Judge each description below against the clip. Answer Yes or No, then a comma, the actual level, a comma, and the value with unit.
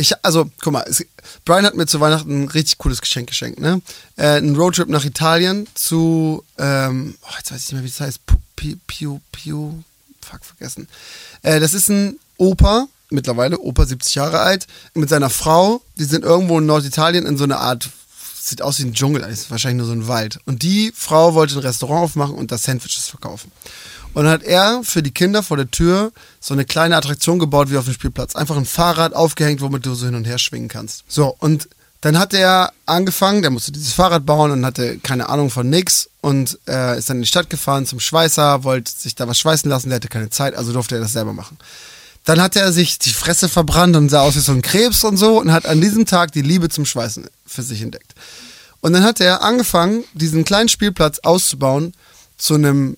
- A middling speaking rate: No, fast, 220 wpm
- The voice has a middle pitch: Yes, medium, 150 Hz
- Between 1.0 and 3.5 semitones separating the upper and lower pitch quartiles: No, average, 4.5 semitones